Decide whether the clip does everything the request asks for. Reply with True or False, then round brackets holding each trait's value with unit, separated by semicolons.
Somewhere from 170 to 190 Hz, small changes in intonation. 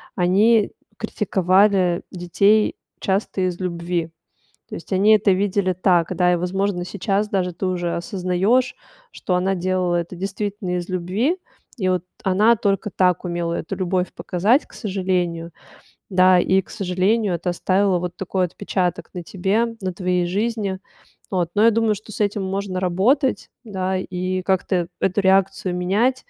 True (185 Hz; 2.1 semitones)